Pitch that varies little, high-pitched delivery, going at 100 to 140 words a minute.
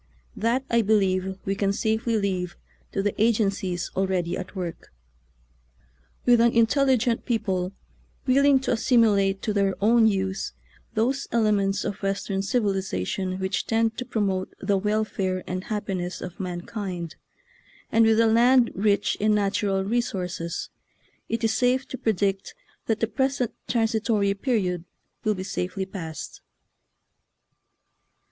No: average, 3.1 semitones; high, 205 Hz; slow, 135 wpm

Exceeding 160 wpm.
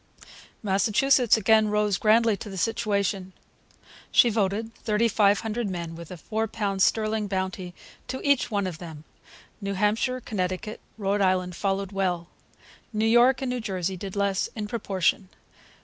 No: average, 150 wpm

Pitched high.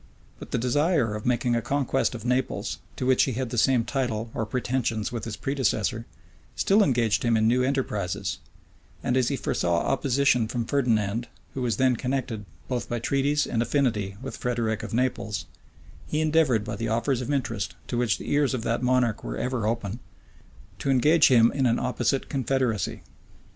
No: low, 125 Hz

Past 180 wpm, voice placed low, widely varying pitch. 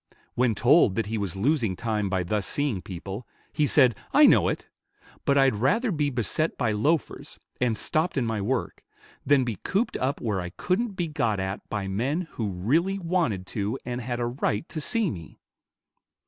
Yes: average, 190 wpm; low, 120 Hz; wide, 6.5 semitones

